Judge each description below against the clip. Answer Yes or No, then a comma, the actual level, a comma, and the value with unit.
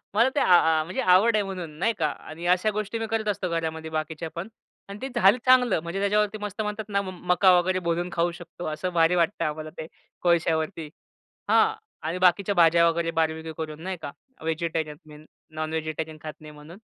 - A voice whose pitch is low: No, medium, 170 Hz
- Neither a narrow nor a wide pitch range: Yes, average, 3.8 semitones